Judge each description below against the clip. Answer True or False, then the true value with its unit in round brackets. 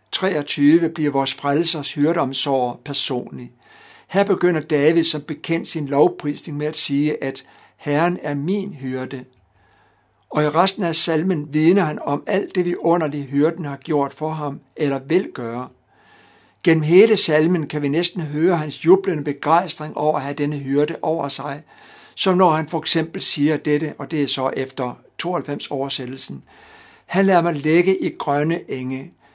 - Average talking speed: True (160 wpm)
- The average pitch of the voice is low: False (155 Hz)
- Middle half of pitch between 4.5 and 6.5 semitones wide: False (3.4 semitones)